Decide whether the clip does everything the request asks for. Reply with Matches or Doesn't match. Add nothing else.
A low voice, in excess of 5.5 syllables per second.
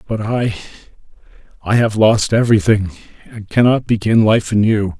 Doesn't match